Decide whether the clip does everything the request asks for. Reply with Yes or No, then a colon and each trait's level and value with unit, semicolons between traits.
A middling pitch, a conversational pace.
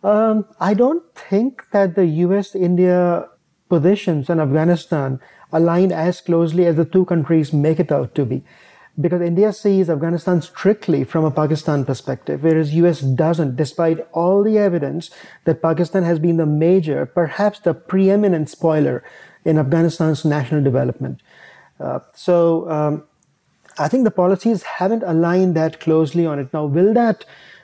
Yes: medium, 170 Hz; average, 150 wpm